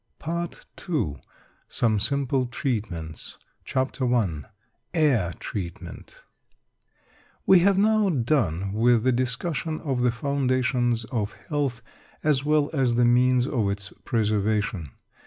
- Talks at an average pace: No, slow, 115 wpm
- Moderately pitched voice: No, low, 125 Hz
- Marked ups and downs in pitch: No, average, 4.7 semitones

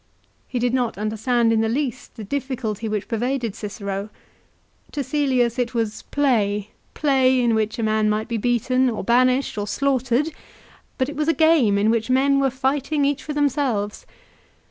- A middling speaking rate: Yes, average, 175 wpm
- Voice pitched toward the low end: No, high, 245 Hz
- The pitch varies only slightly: No, average, 3.8 semitones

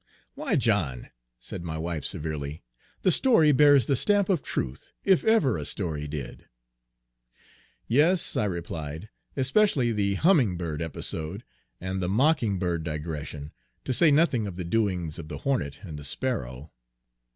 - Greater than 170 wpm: No, average, 150 wpm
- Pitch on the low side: Yes, very low, 95 Hz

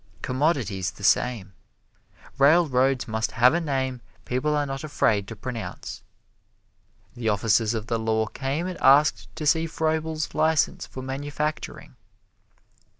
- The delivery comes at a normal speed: No, slow, 130 wpm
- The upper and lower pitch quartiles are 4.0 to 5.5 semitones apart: Yes, average, 5.1 semitones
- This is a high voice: No, low, 135 Hz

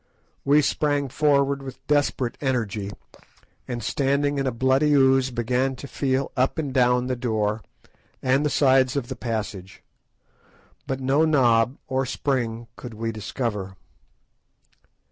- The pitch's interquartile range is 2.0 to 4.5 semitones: Yes, average, 2.9 semitones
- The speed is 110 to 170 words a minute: Yes, slow, 135 wpm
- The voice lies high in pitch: No, low, 130 Hz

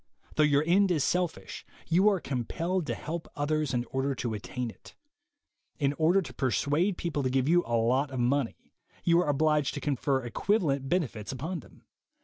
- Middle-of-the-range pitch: Yes, medium, 145 Hz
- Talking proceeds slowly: No, average, 185 wpm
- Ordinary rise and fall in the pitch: Yes, average, 4.6 semitones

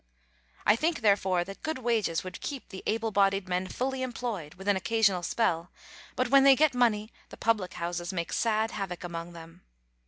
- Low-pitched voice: No, high, 205 Hz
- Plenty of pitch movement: No, average, 4.8 semitones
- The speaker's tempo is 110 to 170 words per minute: No, average, 185 wpm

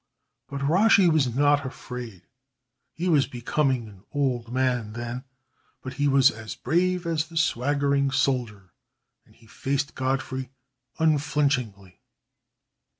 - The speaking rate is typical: No, slow, 120 wpm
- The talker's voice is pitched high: No, low, 135 Hz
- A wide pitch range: No, average, 3.2 semitones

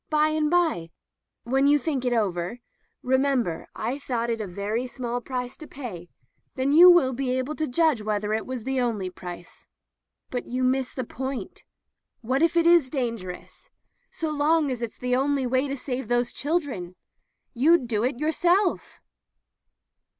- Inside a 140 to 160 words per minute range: No, average, 180 wpm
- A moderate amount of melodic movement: Yes, average, 3.8 semitones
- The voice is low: No, very high, 255 Hz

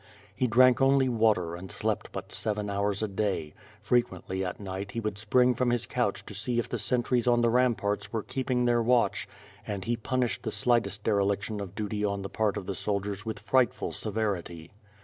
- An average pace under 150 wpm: No, average, 195 wpm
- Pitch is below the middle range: Yes, low, 105 Hz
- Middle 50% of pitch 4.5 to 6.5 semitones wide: No, average, 3.2 semitones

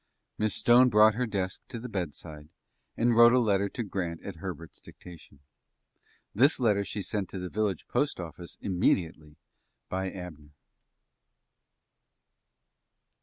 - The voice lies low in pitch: Yes, very low, 95 Hz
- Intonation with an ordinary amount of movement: Yes, average, 4.0 semitones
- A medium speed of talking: No, slow, 125 wpm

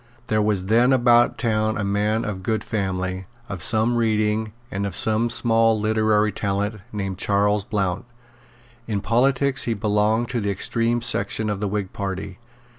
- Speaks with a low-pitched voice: Yes, low, 105 Hz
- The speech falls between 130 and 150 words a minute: No, average, 160 wpm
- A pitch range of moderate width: No, narrow, 2.2 semitones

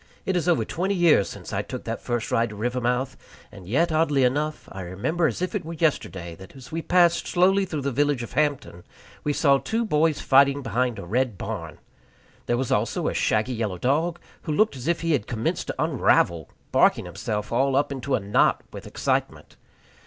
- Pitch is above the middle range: No, medium, 140 Hz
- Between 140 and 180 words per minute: No, fast, 205 wpm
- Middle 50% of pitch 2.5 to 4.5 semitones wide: No, wide, 5.6 semitones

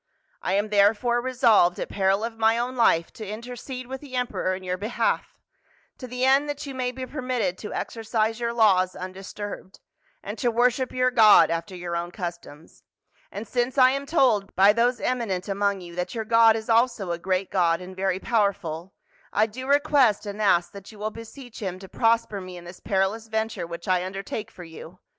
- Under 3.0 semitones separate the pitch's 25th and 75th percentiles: No, average, 4.6 semitones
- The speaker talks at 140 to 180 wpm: No, average, 200 wpm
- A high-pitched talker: Yes, high, 215 Hz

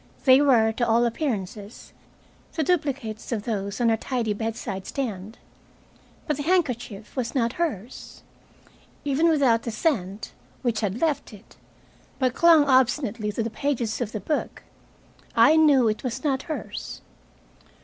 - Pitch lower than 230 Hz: No, high, 240 Hz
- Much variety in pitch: No, average, 4.5 semitones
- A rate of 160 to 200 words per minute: No, average, 145 wpm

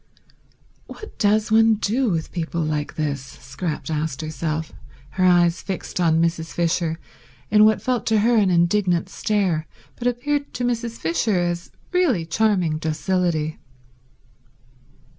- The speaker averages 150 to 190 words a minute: No, slow, 135 wpm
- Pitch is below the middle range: No, medium, 175 Hz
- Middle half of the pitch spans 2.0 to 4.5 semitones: No, average, 5.1 semitones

